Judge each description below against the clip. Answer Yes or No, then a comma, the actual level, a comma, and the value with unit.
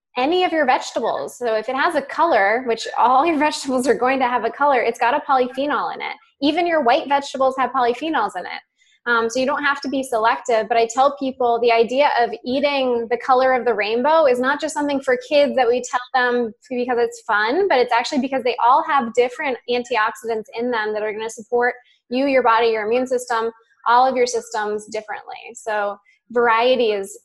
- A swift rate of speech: Yes, fast, 215 wpm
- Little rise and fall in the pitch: No, average, 3.3 semitones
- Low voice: No, very high, 250 Hz